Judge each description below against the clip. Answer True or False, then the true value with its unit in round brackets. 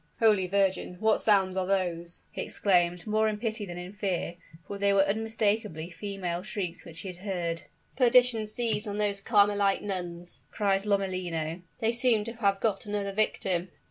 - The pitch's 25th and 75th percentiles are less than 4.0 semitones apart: True (3.0 semitones)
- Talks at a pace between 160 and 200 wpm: True (165 wpm)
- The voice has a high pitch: True (200 Hz)